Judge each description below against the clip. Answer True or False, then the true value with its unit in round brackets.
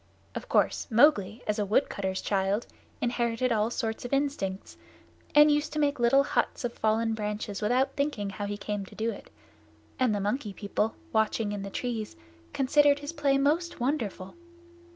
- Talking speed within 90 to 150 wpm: False (165 wpm)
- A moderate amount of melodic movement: True (4.9 semitones)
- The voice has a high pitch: True (230 Hz)